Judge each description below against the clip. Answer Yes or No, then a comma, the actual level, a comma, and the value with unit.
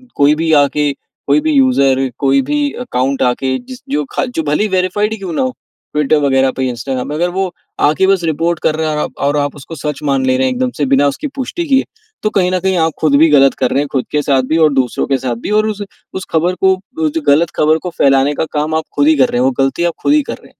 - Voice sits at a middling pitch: Yes, medium, 150 Hz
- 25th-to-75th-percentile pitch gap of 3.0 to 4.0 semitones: No, average, 5.3 semitones